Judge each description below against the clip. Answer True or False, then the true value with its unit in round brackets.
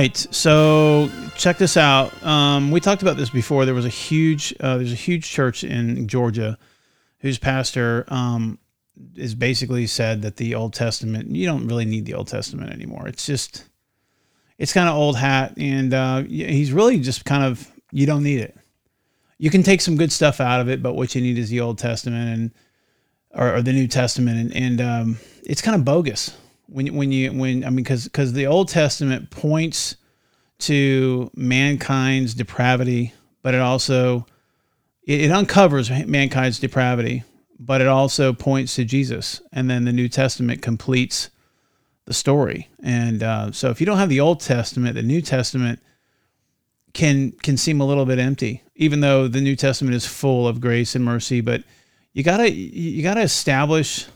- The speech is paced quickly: False (180 wpm)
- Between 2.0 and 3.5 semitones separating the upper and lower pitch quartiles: True (2.8 semitones)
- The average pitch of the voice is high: False (130 Hz)